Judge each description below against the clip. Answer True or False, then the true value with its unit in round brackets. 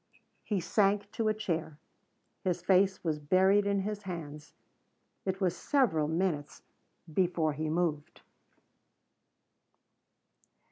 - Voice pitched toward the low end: False (180 Hz)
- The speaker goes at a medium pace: False (105 wpm)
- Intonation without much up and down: False (4.0 semitones)